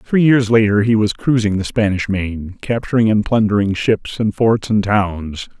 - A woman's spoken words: No, male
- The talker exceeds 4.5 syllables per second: No, 4.4 syllables/s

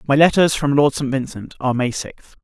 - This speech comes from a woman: No, male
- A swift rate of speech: Yes, fast, 220 wpm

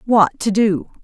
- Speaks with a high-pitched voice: Yes, high, 205 Hz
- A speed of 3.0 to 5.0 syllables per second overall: Yes, 3.8 syllables/s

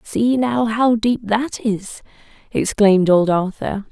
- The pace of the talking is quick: No, average, 140 wpm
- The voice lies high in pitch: Yes, high, 215 Hz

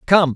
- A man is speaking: Yes, male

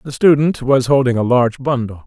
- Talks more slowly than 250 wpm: Yes, fast, 205 wpm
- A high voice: No, low, 130 Hz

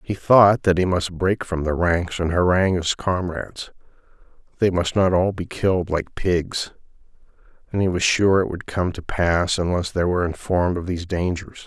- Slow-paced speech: No, average, 190 wpm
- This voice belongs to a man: Yes, male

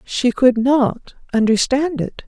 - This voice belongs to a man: No, female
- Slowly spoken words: Yes, slow, 130 wpm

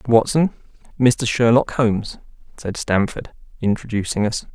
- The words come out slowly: Yes, slow, 120 wpm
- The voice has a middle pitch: No, low, 115 Hz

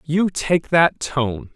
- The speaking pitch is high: No, medium, 150 Hz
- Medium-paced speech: Yes, average, 155 wpm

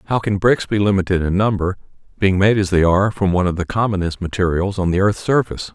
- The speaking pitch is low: Yes, very low, 95 Hz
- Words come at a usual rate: No, fast, 230 wpm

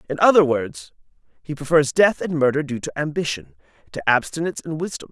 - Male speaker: Yes, male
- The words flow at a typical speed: Yes, average, 175 wpm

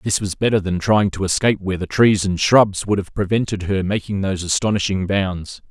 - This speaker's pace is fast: Yes, fast, 210 wpm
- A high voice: No, low, 100 Hz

